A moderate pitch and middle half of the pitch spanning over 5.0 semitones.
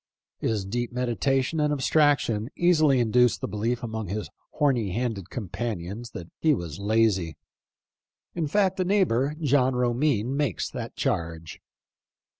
No: low, 120 Hz; wide, 5.5 semitones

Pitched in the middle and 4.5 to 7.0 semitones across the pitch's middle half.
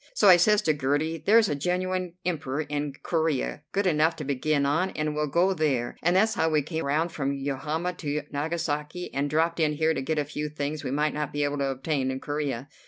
No: medium, 150 Hz; narrow, 2.6 semitones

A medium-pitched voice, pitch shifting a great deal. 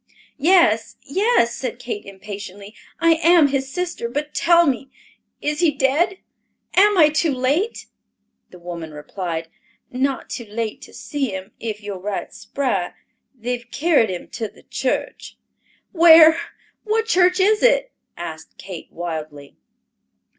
No: very high, 260 Hz; wide, 8.9 semitones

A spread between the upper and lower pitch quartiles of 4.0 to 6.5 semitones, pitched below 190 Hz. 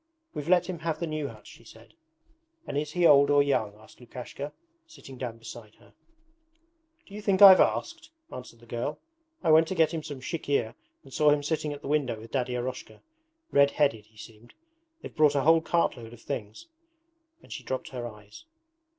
Yes: average, 5.0 semitones; medium, 140 Hz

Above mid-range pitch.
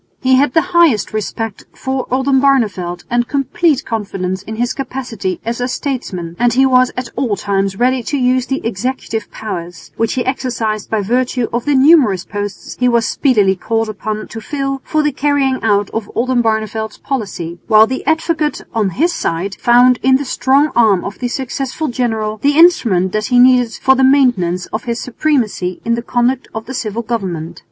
Yes: high, 240 Hz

